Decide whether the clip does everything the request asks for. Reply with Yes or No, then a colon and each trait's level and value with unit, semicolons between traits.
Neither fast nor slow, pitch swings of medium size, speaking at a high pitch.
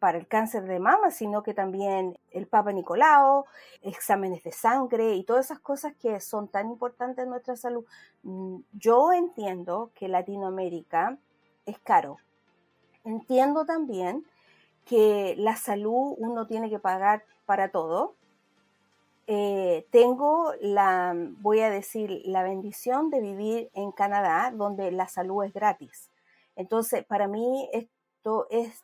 Yes: average, 135 wpm; average, 4.1 semitones; high, 215 Hz